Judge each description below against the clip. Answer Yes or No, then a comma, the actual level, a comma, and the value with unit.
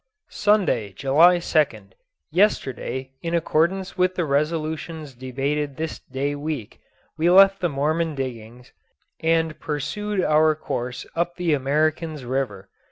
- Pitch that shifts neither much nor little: Yes, average, 4.0 semitones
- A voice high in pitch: No, medium, 155 Hz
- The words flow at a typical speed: No, slow, 120 wpm